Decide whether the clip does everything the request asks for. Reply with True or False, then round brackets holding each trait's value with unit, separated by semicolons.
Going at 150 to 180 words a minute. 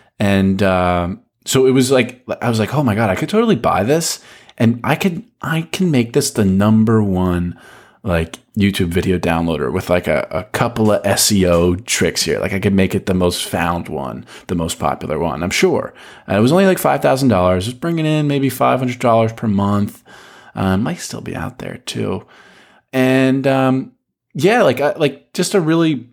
False (190 wpm)